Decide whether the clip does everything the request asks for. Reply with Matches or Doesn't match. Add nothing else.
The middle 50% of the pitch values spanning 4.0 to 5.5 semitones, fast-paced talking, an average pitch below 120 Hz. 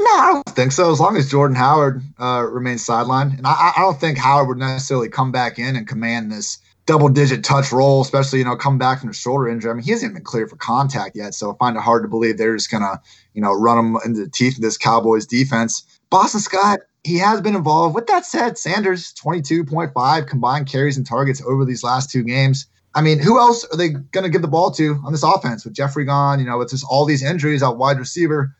Doesn't match